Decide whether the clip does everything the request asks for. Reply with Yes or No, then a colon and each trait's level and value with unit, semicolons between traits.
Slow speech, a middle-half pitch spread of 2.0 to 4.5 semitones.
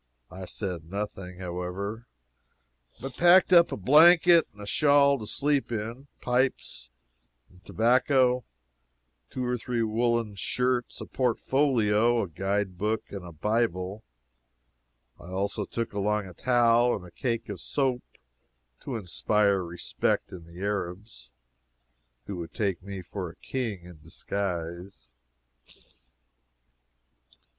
No: slow, 125 wpm; average, 5.2 semitones